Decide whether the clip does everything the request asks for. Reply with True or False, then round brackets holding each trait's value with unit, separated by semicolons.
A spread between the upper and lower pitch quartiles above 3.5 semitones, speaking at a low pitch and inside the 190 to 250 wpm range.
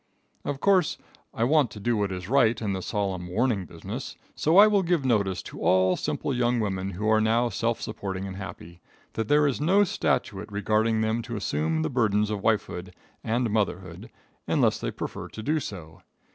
True (4.1 semitones; 110 Hz; 195 wpm)